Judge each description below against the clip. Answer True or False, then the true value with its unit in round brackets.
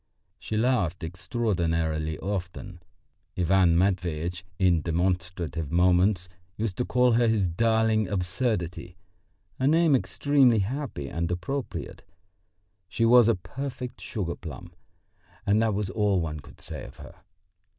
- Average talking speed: False (125 wpm)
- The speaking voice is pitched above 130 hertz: False (95 Hz)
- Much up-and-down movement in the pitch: False (4.8 semitones)